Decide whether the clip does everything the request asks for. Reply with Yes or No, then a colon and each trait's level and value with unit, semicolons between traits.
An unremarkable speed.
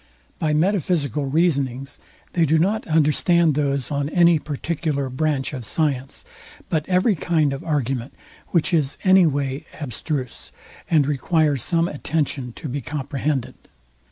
No: slow, 130 wpm